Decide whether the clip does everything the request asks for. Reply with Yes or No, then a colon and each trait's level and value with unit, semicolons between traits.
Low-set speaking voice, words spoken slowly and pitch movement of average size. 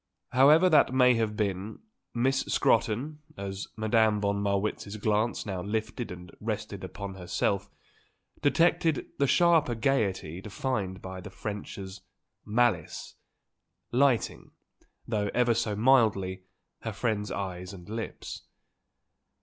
Yes: low, 105 Hz; slow, 115 wpm; average, 3.8 semitones